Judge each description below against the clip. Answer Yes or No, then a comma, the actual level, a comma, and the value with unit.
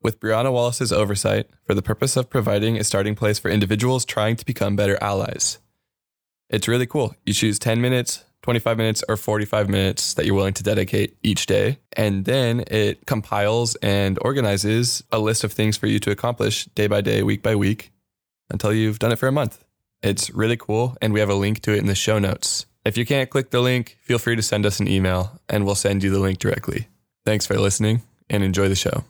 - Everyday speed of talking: No, fast, 220 wpm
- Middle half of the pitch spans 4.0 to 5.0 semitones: No, average, 2.7 semitones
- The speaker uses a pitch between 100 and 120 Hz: Yes, low, 110 Hz